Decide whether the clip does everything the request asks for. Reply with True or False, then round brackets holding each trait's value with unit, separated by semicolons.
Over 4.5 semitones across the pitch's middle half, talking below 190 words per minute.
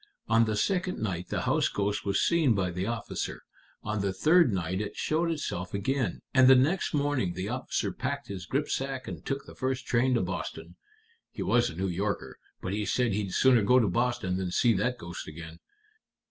False (5.6 semitones; 200 wpm)